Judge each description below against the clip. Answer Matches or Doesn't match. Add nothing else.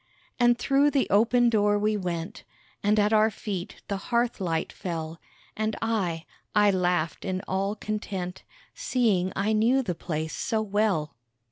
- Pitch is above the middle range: Matches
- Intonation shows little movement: Doesn't match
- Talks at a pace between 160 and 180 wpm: Doesn't match